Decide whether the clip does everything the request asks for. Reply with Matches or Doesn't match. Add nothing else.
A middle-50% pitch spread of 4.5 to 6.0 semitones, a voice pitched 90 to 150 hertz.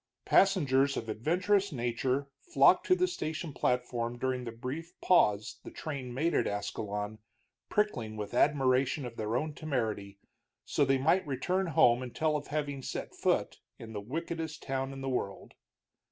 Matches